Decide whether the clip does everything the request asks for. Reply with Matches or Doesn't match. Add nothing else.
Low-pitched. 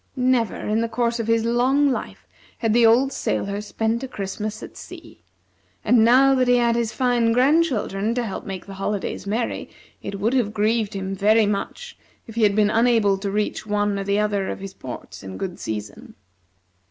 Doesn't match